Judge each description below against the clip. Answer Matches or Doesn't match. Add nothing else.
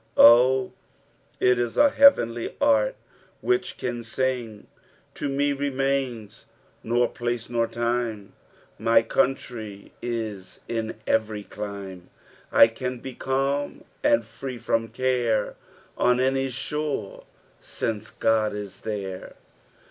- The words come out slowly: Matches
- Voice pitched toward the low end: Matches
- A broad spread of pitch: Doesn't match